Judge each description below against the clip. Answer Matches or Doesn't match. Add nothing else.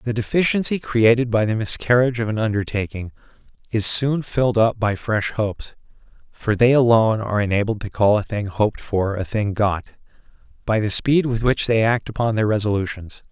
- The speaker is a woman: Doesn't match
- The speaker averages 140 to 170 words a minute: Doesn't match